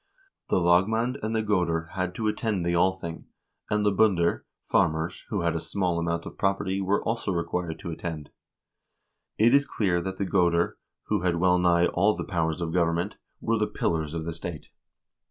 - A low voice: Yes, very low, 90 Hz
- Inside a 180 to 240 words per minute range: Yes, average, 185 wpm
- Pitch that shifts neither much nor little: Yes, average, 3.3 semitones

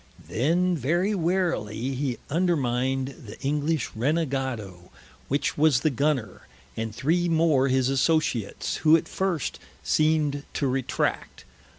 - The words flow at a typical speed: No, slow, 115 wpm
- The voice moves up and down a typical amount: Yes, average, 4.2 semitones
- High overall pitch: No, medium, 140 Hz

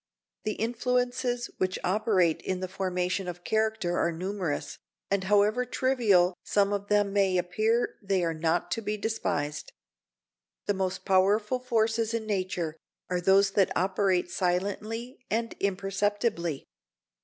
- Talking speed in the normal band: No, slow, 130 wpm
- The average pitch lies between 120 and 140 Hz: No, high, 200 Hz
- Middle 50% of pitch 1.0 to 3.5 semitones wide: Yes, average, 3.2 semitones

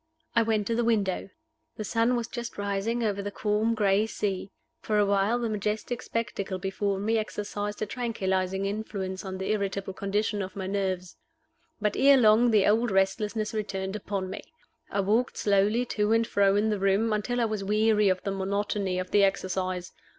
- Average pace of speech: Yes, average, 185 wpm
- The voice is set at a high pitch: Yes, high, 205 Hz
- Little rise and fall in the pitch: Yes, narrow, 2.2 semitones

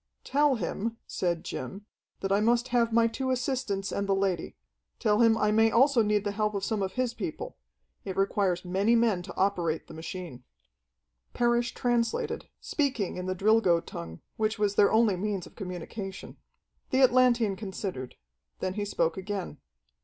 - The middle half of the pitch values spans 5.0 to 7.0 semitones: No, average, 3.7 semitones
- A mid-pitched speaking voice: No, high, 205 Hz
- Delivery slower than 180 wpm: Yes, average, 170 wpm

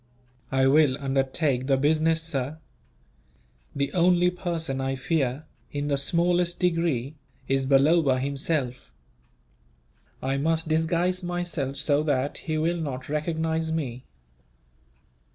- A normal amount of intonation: Yes, average, 3.5 semitones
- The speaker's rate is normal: No, slow, 115 wpm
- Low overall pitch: No, medium, 150 Hz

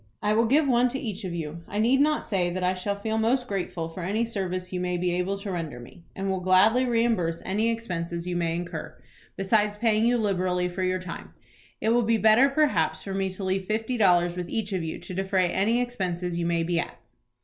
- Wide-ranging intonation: No, average, 4.0 semitones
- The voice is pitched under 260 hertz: Yes, high, 190 Hz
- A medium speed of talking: No, fast, 230 wpm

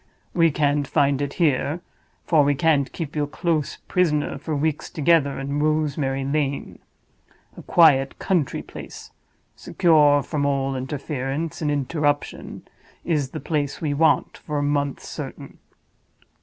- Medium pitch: Yes, medium, 145 Hz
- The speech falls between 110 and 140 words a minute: Yes, slow, 135 wpm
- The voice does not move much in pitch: Yes, narrow, 1.9 semitones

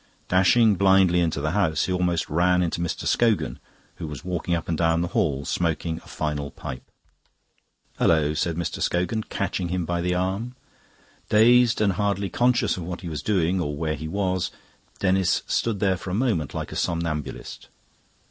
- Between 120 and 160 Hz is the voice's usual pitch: No, very low, 90 Hz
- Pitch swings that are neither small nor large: Yes, average, 3.1 semitones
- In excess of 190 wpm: No, average, 175 wpm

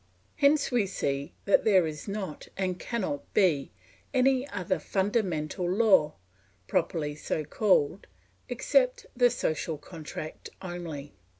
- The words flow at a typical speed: No, slow, 115 wpm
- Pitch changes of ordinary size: No, wide, 6.0 semitones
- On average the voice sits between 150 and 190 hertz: Yes, medium, 185 Hz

